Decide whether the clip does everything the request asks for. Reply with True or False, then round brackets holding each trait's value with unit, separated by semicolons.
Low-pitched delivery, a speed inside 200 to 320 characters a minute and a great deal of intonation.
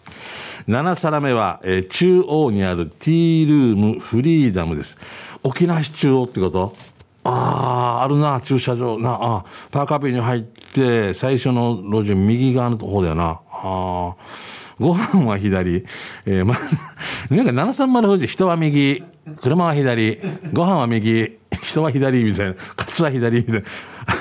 True (125 Hz; 255 characters per minute; 6.7 semitones)